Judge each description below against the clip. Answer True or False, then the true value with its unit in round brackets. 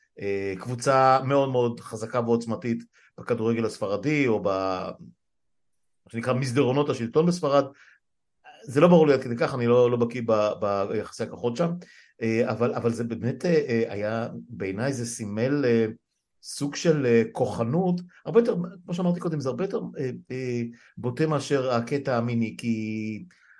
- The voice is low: True (120 Hz)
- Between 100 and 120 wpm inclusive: False (130 wpm)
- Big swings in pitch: False (3.8 semitones)